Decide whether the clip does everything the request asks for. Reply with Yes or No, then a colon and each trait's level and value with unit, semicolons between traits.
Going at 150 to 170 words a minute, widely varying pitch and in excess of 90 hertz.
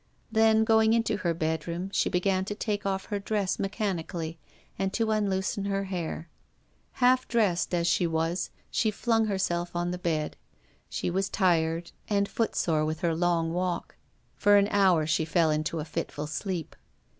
No: average, 165 wpm; average, 3.5 semitones; medium, 185 Hz